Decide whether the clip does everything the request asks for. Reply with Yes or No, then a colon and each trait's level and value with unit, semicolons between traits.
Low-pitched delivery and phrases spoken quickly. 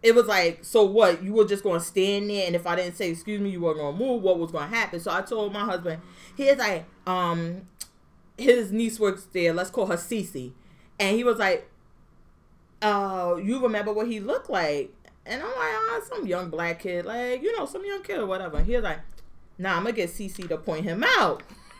No: high, 200 Hz; fast, 230 wpm